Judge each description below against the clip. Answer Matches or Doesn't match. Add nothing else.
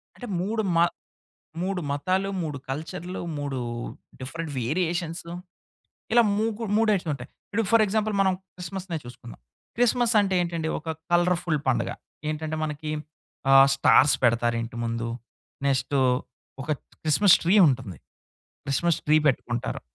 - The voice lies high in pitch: Doesn't match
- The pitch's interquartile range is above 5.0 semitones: Matches